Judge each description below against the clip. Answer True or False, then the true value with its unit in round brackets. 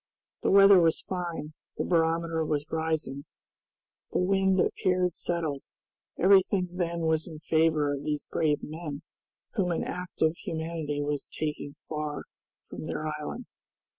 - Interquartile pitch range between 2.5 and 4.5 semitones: True (2.8 semitones)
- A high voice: False (160 Hz)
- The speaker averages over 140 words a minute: False (135 wpm)